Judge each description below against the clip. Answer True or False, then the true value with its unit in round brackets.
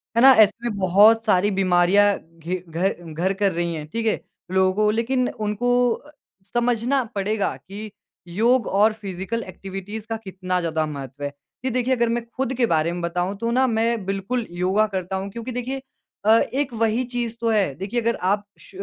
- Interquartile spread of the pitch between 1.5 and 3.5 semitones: False (3.9 semitones)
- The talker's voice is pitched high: True (210 Hz)